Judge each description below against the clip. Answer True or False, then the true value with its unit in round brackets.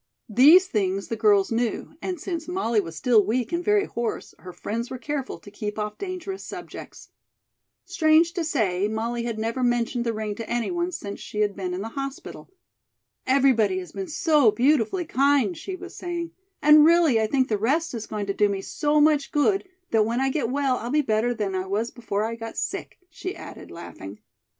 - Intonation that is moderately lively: False (6.3 semitones)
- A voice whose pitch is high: True (240 Hz)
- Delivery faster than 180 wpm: True (200 wpm)